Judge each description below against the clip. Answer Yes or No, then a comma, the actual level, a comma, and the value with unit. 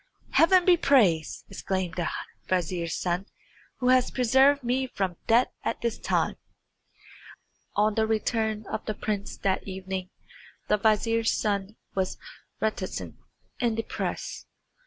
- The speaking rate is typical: No, slow, 130 wpm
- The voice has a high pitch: Yes, high, 215 Hz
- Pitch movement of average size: Yes, average, 4.0 semitones